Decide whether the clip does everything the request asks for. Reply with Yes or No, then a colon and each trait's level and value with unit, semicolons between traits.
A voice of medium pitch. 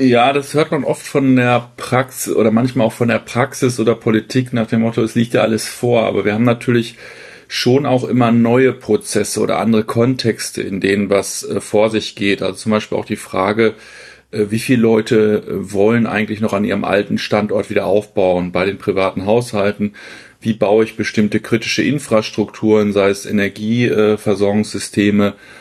No: low, 110 Hz